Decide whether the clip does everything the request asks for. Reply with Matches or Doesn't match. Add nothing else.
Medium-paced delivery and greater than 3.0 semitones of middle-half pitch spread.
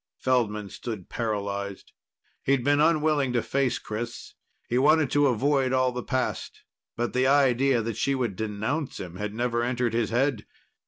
Matches